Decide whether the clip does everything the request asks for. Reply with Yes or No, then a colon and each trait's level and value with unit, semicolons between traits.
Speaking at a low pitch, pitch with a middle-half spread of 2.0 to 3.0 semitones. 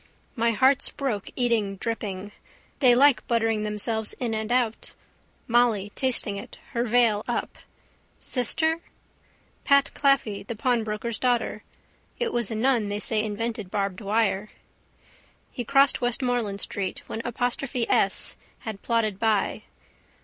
No: high, 230 Hz; average, 2.7 semitones